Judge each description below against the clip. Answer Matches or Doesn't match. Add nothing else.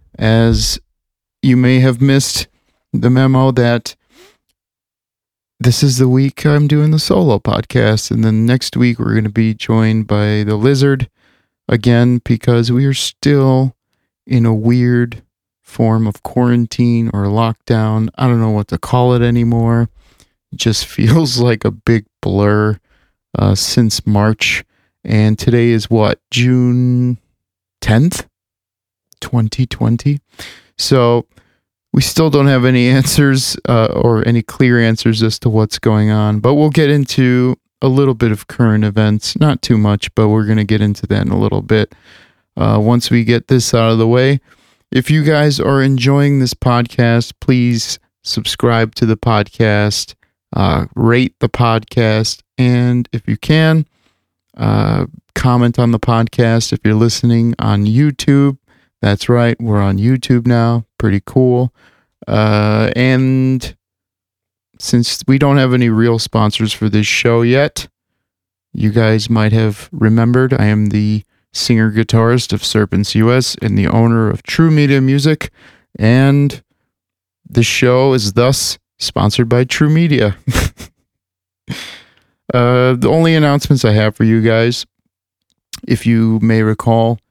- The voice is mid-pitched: Doesn't match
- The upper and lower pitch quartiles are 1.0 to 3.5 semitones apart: Matches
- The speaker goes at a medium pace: Matches